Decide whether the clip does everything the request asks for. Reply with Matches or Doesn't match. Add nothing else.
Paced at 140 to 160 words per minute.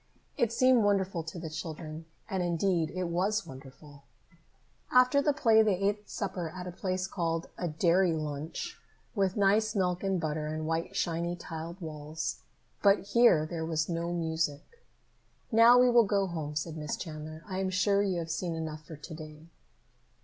Doesn't match